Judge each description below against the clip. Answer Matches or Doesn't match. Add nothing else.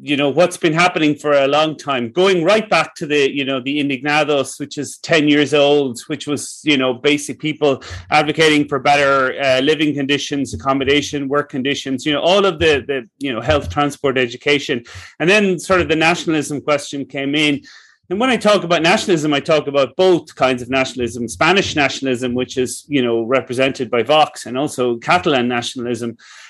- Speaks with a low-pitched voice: Doesn't match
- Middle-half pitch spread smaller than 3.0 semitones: Matches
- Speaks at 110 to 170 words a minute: Doesn't match